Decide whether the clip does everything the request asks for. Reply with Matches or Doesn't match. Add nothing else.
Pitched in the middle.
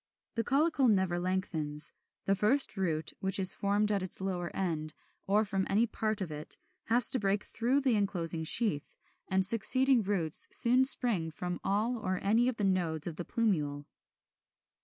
Doesn't match